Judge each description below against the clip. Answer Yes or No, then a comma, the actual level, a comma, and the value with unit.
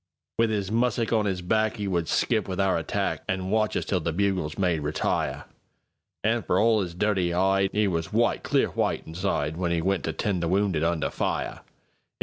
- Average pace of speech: Yes, average, 175 wpm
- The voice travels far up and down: No, average, 3.7 semitones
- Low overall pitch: Yes, very low, 95 Hz